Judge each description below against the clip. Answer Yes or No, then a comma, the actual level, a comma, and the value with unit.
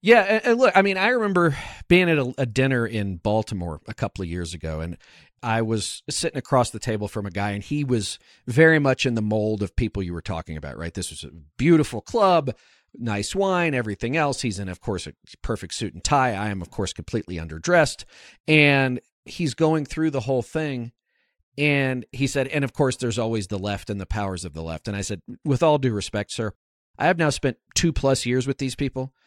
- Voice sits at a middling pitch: No, low, 120 Hz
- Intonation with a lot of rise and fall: Yes, wide, 6.0 semitones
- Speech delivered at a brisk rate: Yes, fast, 220 wpm